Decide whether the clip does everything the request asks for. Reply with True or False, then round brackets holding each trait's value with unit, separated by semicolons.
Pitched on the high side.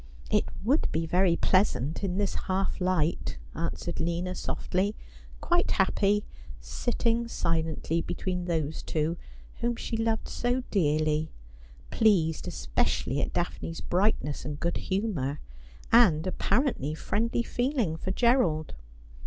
False (180 Hz)